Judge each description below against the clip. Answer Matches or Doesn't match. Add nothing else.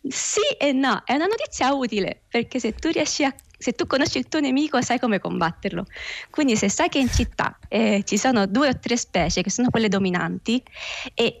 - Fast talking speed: Matches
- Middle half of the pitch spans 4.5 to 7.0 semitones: Matches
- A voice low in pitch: Doesn't match